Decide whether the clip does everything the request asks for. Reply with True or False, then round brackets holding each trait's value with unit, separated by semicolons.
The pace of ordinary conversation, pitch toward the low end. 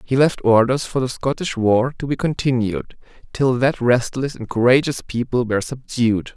True (170 wpm; 125 Hz)